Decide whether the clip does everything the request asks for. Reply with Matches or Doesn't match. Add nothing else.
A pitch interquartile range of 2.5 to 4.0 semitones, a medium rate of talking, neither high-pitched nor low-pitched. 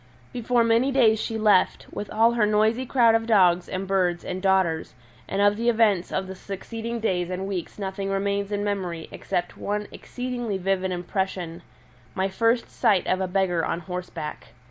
Doesn't match